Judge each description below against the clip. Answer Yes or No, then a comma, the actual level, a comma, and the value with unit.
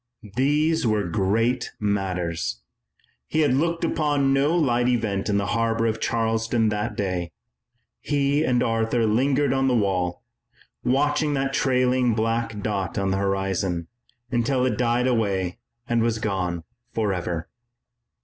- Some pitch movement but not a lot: Yes, average, 4.8 semitones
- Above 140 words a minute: No, slow, 135 wpm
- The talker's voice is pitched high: No, low, 115 Hz